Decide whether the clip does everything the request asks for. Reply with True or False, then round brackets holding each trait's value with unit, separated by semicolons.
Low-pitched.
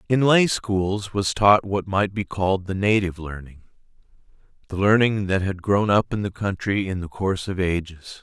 True (95 Hz)